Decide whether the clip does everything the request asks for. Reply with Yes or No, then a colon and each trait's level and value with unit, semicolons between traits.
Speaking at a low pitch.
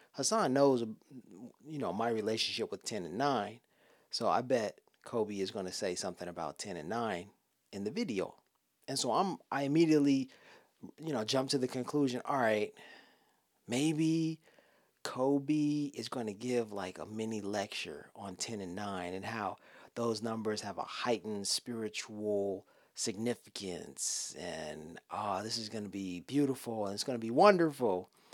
Yes: low, 115 Hz